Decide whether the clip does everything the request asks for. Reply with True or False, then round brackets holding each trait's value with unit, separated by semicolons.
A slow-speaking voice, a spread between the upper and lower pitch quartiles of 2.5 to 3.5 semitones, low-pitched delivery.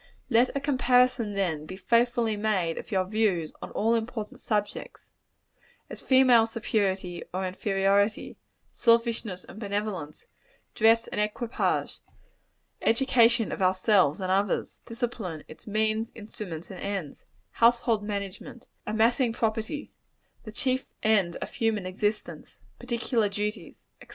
False (120 wpm; 3.1 semitones; 215 Hz)